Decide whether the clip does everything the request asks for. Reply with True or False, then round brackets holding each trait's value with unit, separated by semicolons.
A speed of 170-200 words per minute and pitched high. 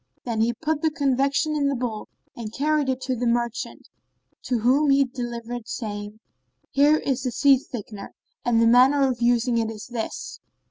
True (185 wpm; 245 Hz)